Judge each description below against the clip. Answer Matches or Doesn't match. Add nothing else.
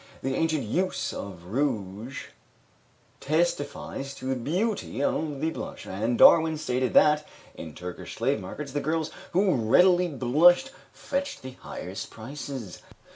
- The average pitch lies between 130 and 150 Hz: Matches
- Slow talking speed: Matches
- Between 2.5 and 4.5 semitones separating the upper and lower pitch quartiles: Doesn't match